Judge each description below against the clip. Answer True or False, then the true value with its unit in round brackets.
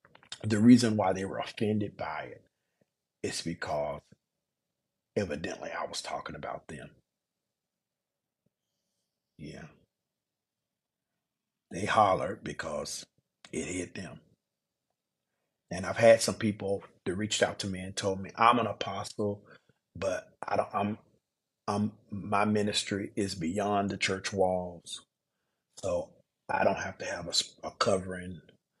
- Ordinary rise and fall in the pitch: False (2.1 semitones)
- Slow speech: True (125 wpm)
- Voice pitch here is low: True (100 Hz)